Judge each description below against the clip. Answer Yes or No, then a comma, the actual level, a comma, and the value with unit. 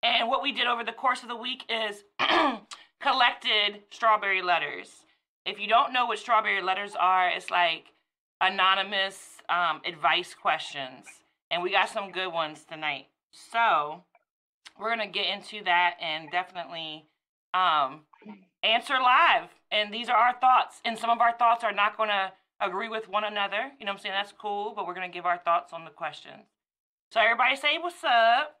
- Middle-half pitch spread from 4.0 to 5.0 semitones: Yes, average, 4.5 semitones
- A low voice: No, high, 205 Hz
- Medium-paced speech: Yes, average, 185 wpm